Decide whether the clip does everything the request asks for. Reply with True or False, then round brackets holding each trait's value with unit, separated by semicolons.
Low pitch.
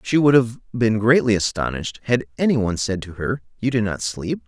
True (110 Hz)